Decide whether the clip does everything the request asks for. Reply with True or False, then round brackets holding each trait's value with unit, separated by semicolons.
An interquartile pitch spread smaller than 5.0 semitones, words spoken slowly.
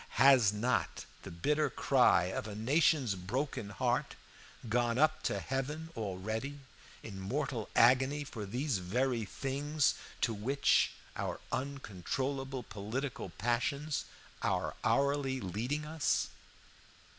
True (4.6 semitones; 110 wpm)